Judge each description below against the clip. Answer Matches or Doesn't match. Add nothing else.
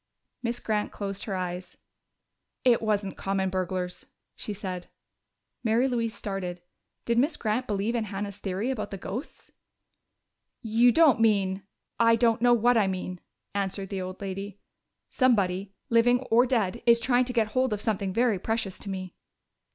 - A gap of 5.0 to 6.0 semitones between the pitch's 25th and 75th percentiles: Doesn't match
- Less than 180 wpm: Matches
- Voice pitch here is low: Doesn't match